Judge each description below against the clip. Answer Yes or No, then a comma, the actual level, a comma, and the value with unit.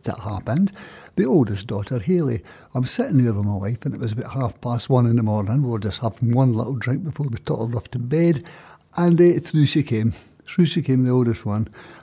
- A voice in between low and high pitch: No, low, 125 Hz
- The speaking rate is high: Yes, fast, 230 wpm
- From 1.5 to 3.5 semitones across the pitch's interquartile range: No, average, 4.5 semitones